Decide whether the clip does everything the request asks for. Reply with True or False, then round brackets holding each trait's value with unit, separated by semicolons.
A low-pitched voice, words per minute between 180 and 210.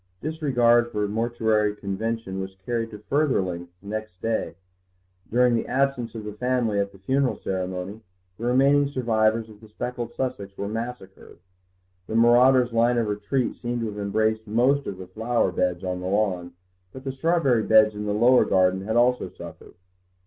False (110 Hz; 170 wpm)